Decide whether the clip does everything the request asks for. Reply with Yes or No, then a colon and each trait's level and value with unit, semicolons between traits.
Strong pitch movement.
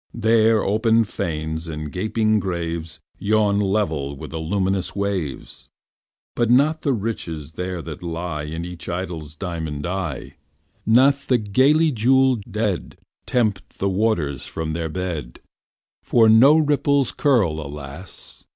Yes: wide, 5.7 semitones